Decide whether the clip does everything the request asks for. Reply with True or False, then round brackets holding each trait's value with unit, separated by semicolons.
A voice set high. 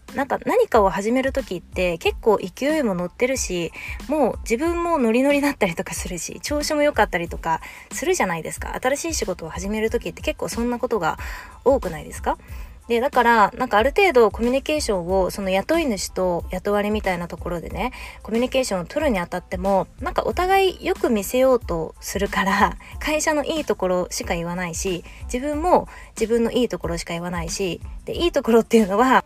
True (230 Hz)